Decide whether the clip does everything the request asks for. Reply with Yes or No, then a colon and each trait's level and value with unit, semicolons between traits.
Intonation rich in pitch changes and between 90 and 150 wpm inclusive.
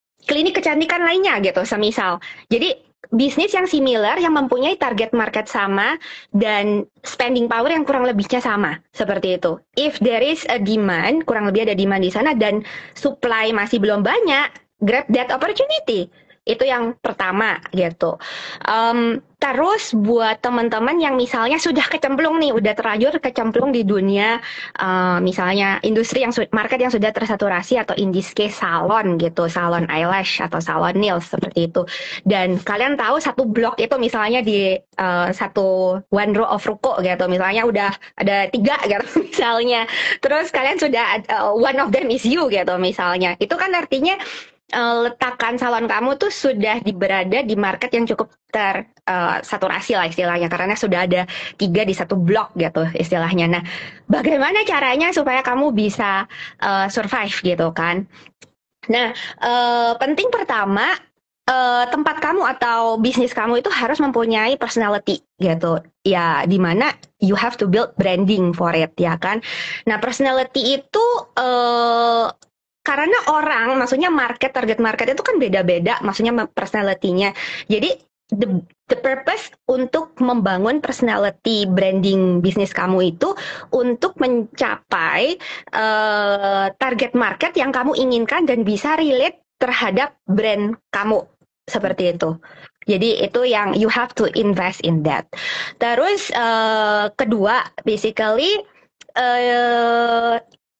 No: average, 4.9 semitones; average, 140 wpm